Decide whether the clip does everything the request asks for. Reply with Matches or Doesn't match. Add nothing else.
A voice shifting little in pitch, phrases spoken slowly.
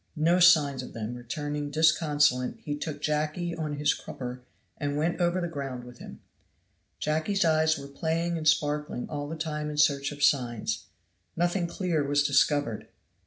Doesn't match